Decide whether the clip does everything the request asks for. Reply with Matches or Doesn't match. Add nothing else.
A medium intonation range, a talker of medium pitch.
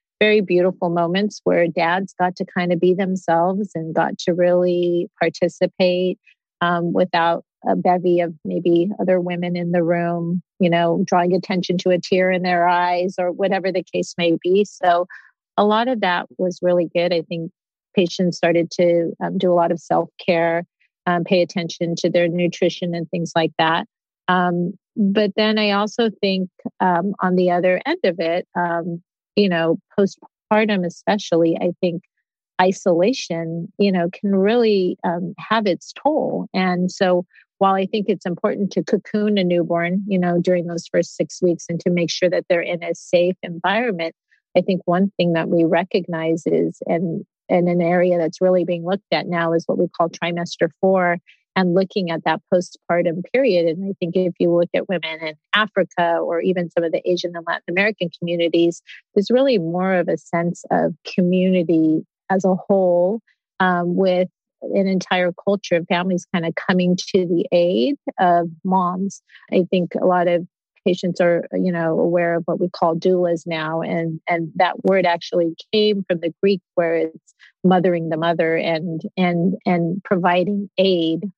Doesn't match